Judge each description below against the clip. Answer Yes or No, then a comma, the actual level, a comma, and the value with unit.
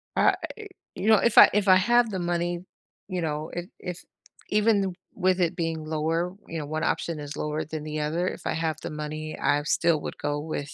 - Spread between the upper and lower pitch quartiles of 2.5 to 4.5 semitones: Yes, average, 3.1 semitones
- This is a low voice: No, medium, 165 Hz